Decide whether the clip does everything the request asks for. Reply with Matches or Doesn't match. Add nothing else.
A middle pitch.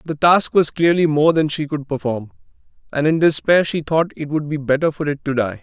Matches